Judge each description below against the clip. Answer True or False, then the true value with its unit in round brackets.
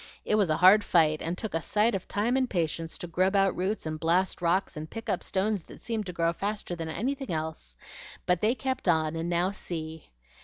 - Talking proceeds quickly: True (225 wpm)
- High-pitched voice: False (180 Hz)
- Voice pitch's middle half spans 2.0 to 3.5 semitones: False (4.3 semitones)